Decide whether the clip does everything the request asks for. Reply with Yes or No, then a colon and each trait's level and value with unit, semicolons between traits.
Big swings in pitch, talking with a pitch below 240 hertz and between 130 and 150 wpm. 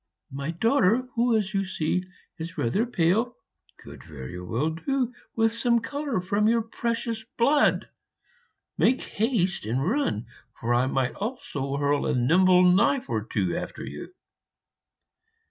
Yes: wide, 8.3 semitones; high, 190 Hz; average, 140 wpm